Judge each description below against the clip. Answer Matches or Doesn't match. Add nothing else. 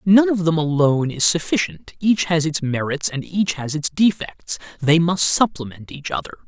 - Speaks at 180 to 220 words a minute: Matches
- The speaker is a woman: Doesn't match